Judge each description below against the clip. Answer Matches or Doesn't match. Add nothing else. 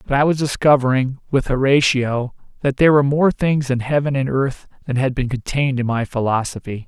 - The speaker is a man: Matches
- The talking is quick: Doesn't match